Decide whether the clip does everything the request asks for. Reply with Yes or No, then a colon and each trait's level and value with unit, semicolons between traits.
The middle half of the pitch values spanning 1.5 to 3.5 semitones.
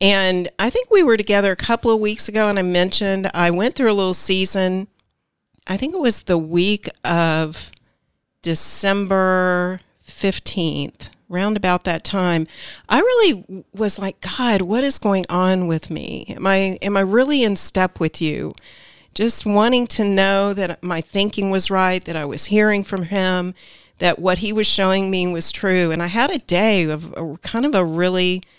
Yes: average, 2.8 semitones